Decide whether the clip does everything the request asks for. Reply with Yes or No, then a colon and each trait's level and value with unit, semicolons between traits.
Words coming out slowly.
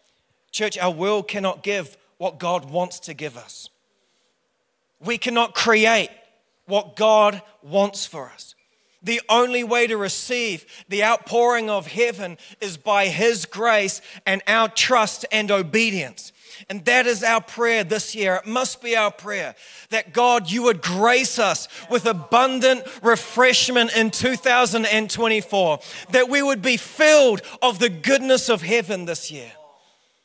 No: average, 145 wpm